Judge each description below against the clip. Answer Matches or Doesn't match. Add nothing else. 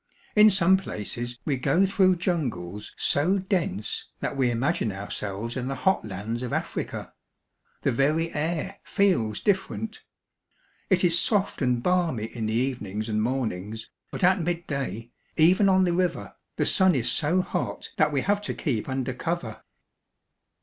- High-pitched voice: Doesn't match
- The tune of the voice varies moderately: Doesn't match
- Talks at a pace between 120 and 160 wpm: Matches